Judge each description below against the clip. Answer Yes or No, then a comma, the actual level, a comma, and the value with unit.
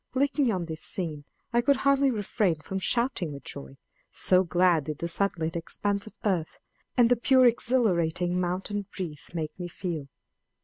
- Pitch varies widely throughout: Yes, wide, 6.1 semitones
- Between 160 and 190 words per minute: Yes, average, 165 wpm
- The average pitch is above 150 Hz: Yes, medium, 185 Hz